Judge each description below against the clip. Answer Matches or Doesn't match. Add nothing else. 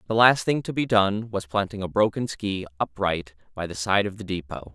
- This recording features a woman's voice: Doesn't match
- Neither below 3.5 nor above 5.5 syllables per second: Matches